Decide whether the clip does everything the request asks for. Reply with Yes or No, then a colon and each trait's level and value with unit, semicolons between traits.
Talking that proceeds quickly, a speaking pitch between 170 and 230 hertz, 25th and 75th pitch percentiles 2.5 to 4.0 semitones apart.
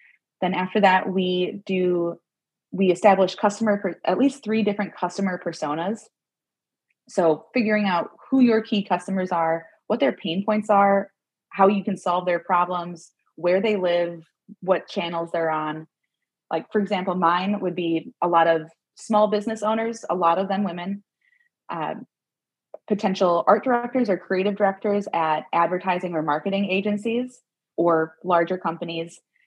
No: average, 150 wpm; high, 190 Hz; average, 3.4 semitones